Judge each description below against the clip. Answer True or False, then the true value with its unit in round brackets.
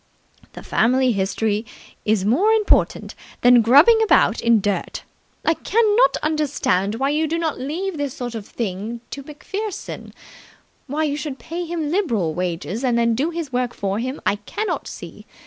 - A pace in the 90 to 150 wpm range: False (165 wpm)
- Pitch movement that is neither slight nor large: False (6.5 semitones)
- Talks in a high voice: True (265 Hz)